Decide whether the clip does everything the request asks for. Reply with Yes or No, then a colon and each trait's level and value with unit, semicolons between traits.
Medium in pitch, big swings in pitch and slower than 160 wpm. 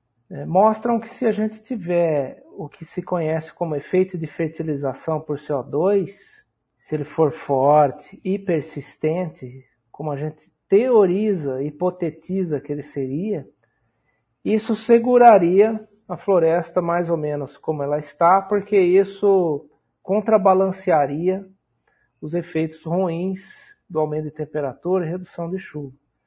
No: medium, 170 Hz; average, 4.5 semitones; average, 125 wpm